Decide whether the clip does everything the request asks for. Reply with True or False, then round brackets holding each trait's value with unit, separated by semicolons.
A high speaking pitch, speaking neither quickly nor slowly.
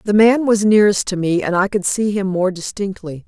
False (195 Hz; 240 wpm)